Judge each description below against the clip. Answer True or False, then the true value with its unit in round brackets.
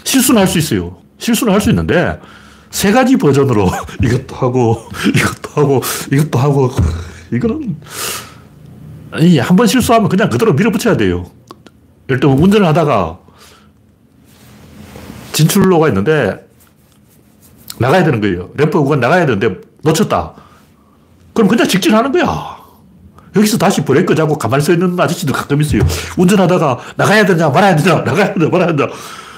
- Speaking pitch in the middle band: True (155 Hz)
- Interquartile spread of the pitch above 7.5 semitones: True (8.1 semitones)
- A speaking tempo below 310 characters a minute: False (325 characters per minute)